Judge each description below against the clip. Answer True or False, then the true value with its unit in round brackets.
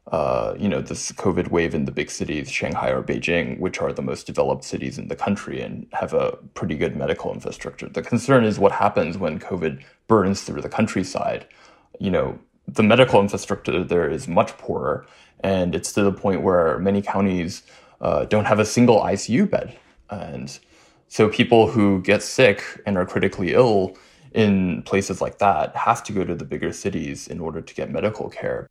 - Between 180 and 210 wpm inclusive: True (190 wpm)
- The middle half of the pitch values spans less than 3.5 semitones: True (2.6 semitones)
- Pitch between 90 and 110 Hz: True (105 Hz)